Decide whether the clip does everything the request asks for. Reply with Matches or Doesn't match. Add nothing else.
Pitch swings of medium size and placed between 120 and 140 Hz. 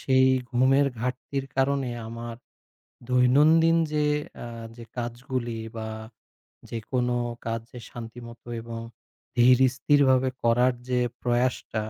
Doesn't match